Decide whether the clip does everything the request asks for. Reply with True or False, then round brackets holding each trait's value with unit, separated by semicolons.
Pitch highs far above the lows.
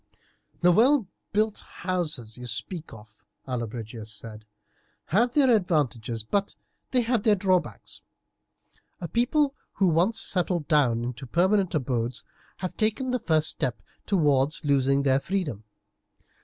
True (8.6 semitones)